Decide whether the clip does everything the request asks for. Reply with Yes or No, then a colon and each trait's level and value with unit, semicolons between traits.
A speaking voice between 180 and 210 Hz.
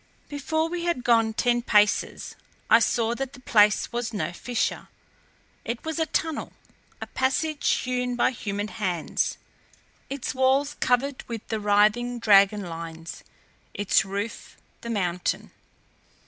No: high, 235 Hz